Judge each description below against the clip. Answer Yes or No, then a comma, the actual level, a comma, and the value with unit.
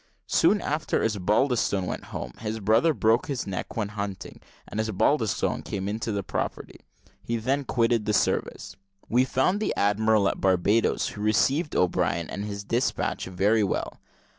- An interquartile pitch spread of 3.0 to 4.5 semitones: No, narrow, 2.6 semitones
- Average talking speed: Yes, average, 155 wpm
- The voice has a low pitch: Yes, low, 105 Hz